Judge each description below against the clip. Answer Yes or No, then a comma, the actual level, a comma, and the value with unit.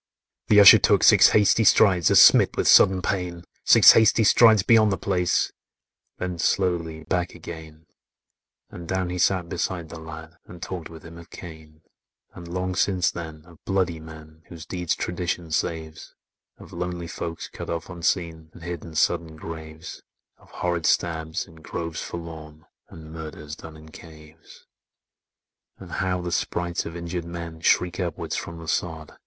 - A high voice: No, very low, 85 Hz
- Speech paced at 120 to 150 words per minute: No, average, 165 wpm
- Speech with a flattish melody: Yes, narrow, 1.9 semitones